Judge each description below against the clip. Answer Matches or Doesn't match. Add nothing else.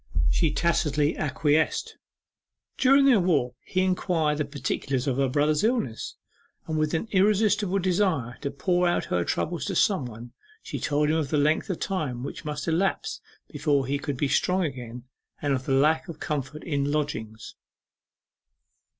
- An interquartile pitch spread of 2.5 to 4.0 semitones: Doesn't match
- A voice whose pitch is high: Doesn't match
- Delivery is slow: Doesn't match